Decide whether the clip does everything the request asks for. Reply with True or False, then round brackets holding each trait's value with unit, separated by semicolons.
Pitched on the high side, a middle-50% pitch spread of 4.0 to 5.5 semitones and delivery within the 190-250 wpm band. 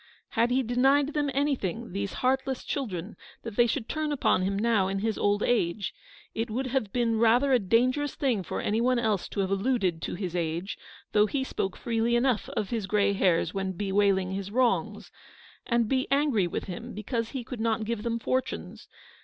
True (225 Hz; 4.3 semitones; 195 wpm)